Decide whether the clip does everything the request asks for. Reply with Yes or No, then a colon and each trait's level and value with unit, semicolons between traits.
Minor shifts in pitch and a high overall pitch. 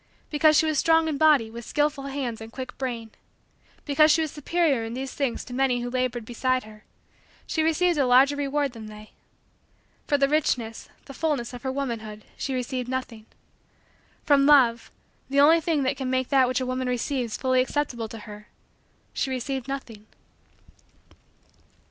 No: average, 3.2 semitones; very high, 260 Hz